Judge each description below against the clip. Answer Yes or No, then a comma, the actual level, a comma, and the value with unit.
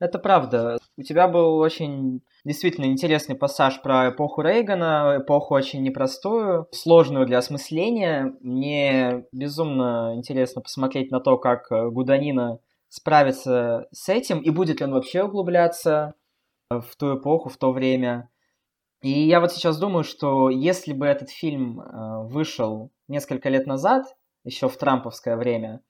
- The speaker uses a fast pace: No, average, 135 wpm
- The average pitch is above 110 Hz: Yes, medium, 140 Hz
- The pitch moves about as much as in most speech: Yes, average, 3.9 semitones